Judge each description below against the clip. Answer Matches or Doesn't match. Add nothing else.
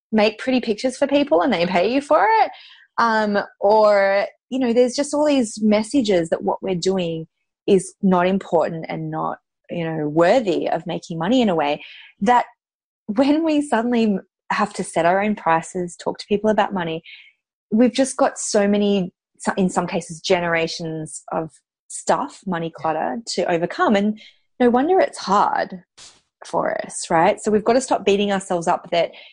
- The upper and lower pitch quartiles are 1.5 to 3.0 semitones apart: Doesn't match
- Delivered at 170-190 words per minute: Matches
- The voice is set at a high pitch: Matches